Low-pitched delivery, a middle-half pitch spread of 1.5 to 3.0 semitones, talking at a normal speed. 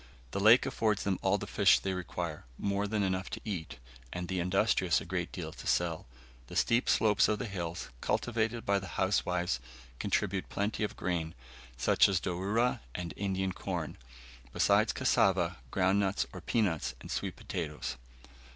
Yes: very low, 95 Hz; narrow, 2.5 semitones; average, 165 wpm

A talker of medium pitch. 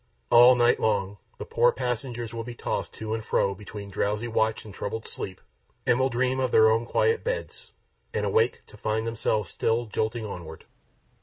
No: low, 115 Hz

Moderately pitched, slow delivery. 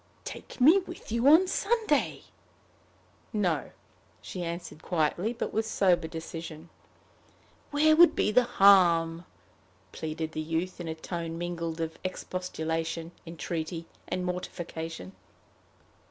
Yes: medium, 175 Hz; slow, 115 wpm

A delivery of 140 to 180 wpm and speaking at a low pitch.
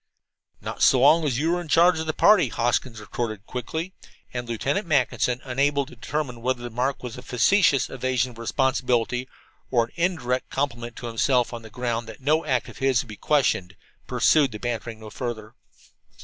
No: average, 190 wpm; low, 125 Hz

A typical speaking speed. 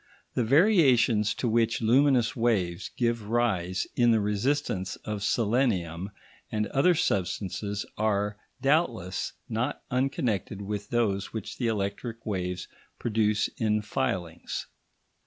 No: slow, 115 wpm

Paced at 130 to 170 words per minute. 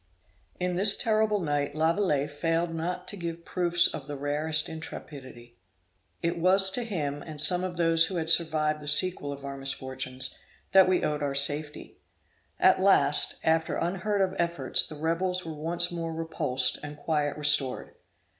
Yes: average, 165 wpm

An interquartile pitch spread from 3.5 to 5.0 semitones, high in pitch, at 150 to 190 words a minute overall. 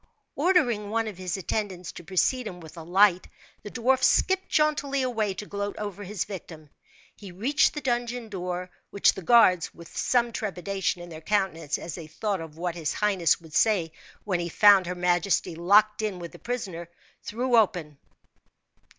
Yes: average, 4.1 semitones; high, 195 Hz; average, 175 wpm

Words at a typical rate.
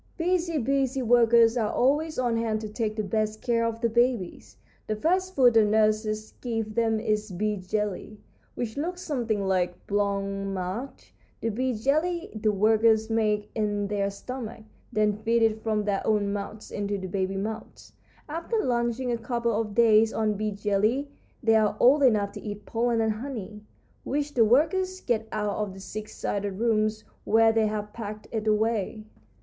Yes: average, 175 wpm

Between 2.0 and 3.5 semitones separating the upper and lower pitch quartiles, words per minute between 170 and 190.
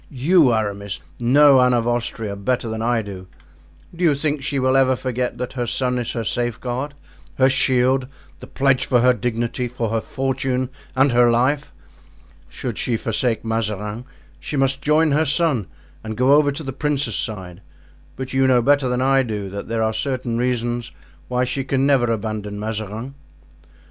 Yes: average, 3.0 semitones; average, 175 wpm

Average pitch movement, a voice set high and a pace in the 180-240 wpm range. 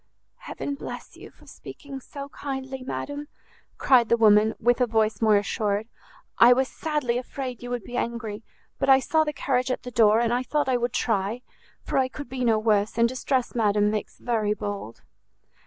Yes: average, 3.3 semitones; high, 240 Hz; average, 190 wpm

